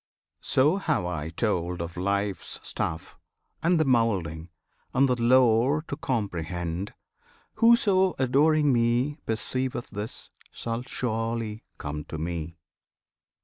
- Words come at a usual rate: No, slow, 110 wpm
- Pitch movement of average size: No, wide, 7.1 semitones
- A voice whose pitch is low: Yes, low, 115 Hz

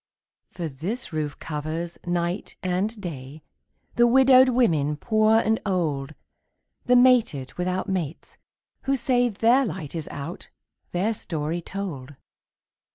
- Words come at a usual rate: No, slow, 120 wpm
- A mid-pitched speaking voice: Yes, medium, 180 Hz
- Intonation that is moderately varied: No, wide, 6.7 semitones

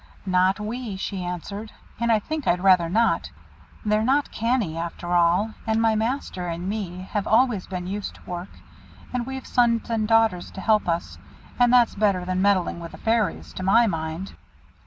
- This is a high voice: Yes, high, 205 Hz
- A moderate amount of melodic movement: Yes, average, 4.1 semitones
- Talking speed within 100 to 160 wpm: No, average, 180 wpm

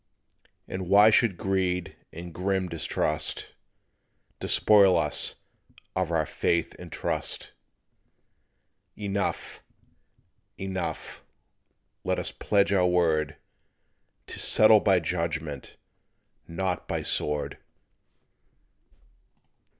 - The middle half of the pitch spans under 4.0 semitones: Yes, average, 2.8 semitones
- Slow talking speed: Yes, slow, 85 wpm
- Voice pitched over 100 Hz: No, very low, 90 Hz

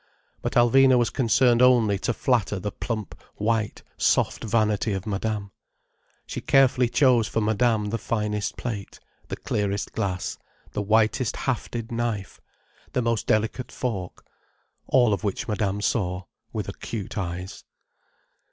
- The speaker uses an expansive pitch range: No, average, 2.8 semitones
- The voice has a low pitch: Yes, low, 110 Hz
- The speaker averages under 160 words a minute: Yes, slow, 135 wpm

